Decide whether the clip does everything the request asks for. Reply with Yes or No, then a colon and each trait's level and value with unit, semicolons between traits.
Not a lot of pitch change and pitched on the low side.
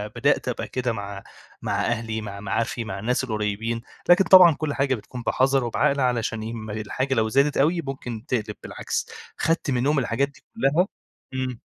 No: average, 3.8 semitones; low, 125 Hz